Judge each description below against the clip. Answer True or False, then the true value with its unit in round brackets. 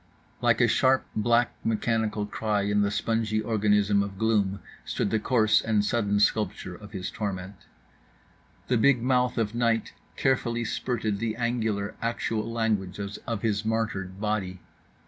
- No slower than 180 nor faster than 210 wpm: False (145 wpm)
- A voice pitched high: False (110 Hz)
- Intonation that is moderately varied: False (2.1 semitones)